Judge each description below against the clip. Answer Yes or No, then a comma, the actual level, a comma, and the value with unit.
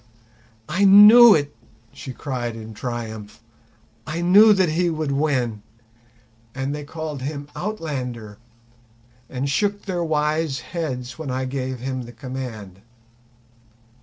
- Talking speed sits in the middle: No, slow, 125 wpm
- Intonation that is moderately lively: Yes, average, 4.7 semitones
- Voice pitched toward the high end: No, medium, 140 Hz